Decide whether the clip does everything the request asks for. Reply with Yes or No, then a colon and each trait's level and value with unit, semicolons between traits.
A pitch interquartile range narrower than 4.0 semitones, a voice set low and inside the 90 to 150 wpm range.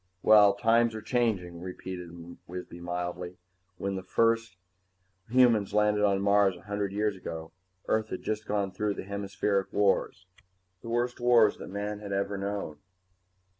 Yes: narrow, 2.4 semitones; low, 100 Hz; average, 145 wpm